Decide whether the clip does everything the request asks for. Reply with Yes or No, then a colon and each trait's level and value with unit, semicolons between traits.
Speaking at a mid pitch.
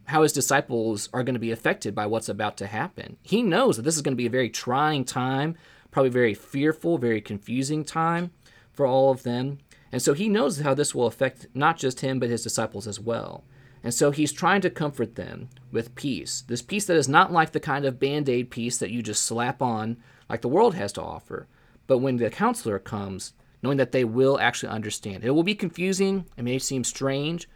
No: low, 130 Hz